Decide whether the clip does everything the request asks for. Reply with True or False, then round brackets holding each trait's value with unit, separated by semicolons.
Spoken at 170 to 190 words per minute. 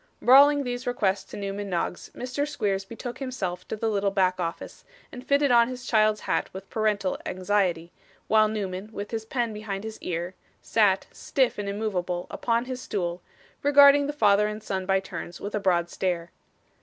True (180 wpm)